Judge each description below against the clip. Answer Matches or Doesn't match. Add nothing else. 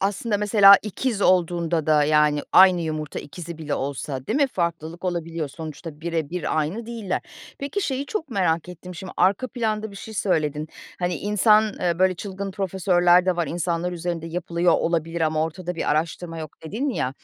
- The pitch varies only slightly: Doesn't match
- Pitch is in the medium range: Matches